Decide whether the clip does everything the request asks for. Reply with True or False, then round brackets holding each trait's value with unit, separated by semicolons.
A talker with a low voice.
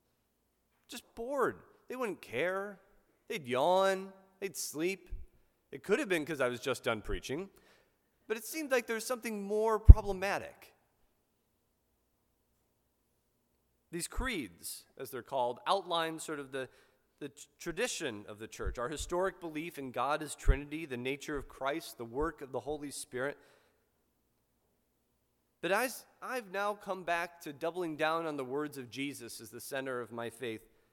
False (160 Hz)